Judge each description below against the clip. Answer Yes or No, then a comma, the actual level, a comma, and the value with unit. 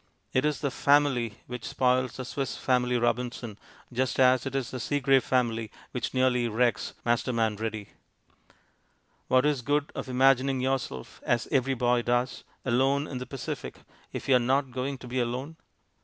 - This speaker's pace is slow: No, average, 170 wpm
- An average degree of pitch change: No, narrow, 1.9 semitones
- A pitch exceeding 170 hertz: No, low, 125 Hz